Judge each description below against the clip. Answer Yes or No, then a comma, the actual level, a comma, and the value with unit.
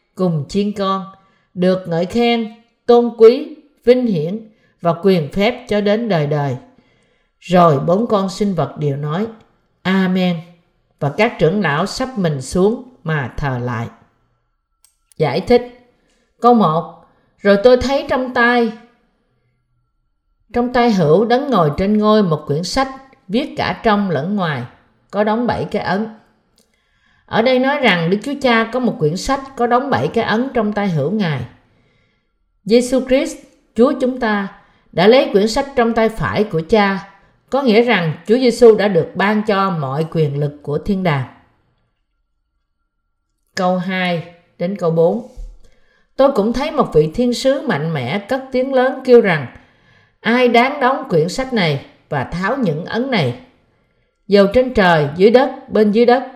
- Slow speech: Yes, slow, 160 wpm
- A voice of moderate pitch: No, high, 205 Hz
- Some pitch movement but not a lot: No, wide, 7.0 semitones